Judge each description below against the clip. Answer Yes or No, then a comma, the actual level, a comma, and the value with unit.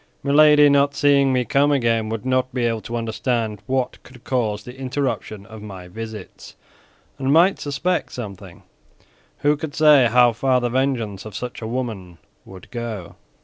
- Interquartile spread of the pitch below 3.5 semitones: No, average, 4.0 semitones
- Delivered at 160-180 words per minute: Yes, average, 165 wpm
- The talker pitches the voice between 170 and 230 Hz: No, low, 125 Hz